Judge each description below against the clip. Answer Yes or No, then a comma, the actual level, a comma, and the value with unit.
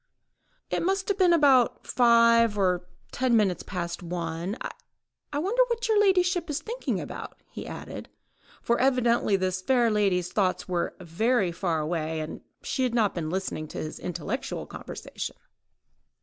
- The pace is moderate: Yes, average, 150 wpm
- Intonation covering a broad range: Yes, wide, 7.1 semitones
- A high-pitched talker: Yes, high, 215 Hz